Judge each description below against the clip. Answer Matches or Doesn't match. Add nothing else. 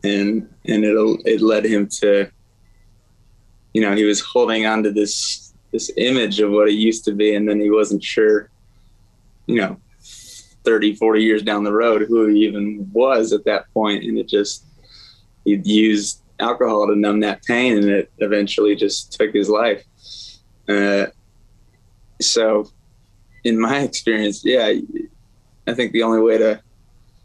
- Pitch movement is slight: Matches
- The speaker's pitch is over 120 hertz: Doesn't match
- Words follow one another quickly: Doesn't match